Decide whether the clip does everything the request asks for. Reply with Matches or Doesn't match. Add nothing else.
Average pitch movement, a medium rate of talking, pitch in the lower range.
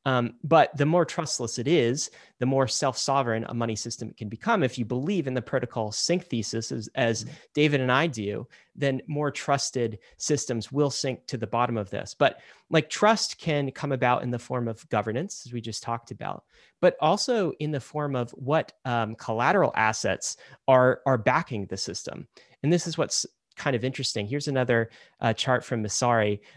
Matches